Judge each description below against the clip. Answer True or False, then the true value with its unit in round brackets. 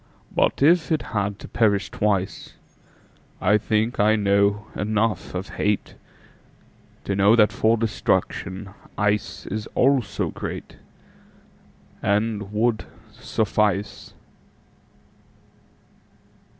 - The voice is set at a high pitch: False (105 Hz)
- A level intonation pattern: True (1.7 semitones)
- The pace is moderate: False (80 wpm)